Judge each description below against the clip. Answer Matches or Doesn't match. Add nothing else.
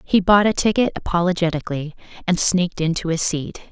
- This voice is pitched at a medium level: Matches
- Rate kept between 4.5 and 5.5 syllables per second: Doesn't match